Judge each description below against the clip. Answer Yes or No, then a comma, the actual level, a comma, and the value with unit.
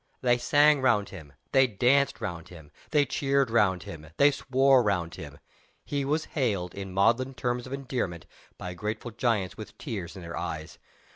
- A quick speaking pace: No, average, 170 wpm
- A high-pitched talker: No, low, 115 Hz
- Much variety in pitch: Yes, wide, 6.8 semitones